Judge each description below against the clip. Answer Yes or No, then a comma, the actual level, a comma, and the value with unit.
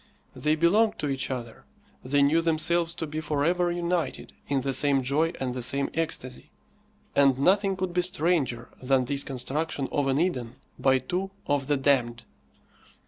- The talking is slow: No, average, 170 wpm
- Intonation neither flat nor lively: Yes, average, 4.1 semitones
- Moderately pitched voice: Yes, medium, 145 Hz